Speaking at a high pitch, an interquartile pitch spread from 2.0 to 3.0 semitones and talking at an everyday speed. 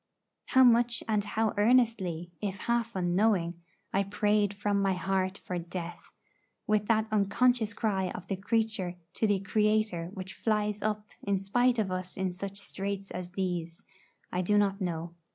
Yes: high, 200 Hz; average, 2.7 semitones; average, 160 wpm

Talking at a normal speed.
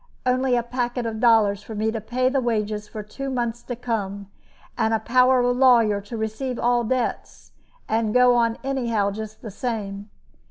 Yes: average, 185 wpm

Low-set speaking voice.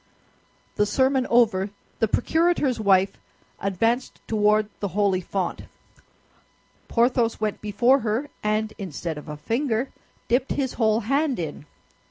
No: high, 220 Hz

